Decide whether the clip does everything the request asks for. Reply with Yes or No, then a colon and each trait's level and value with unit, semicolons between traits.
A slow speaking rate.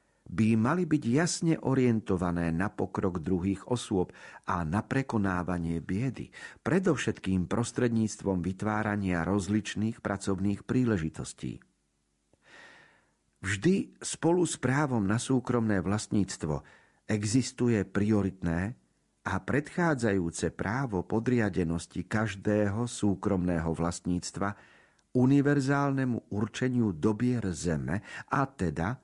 Yes: slow, 85 wpm